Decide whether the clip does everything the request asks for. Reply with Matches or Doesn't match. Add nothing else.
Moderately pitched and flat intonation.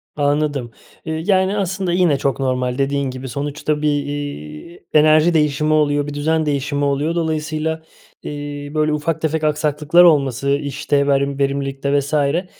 Matches